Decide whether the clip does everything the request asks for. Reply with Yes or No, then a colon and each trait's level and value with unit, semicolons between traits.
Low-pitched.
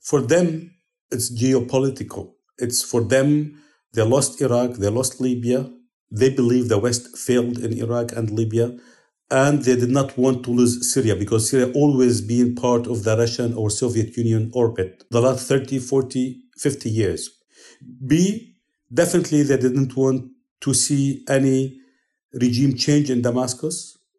Yes: low, 130 Hz